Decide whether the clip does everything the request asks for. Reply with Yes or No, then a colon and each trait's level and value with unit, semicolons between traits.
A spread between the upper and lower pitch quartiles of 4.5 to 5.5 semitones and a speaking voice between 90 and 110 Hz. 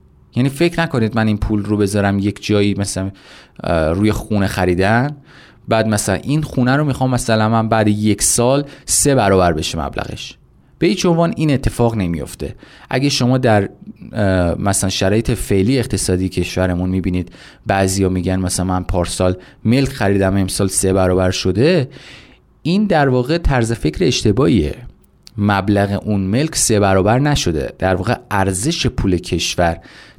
Yes: average, 5.2 semitones; low, 105 Hz